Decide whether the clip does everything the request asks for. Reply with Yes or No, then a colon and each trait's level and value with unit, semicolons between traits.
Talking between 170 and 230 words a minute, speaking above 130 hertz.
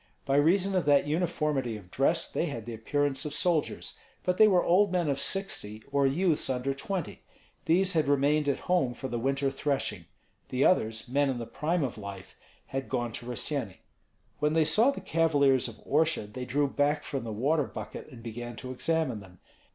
Yes: average, 195 wpm; medium, 140 Hz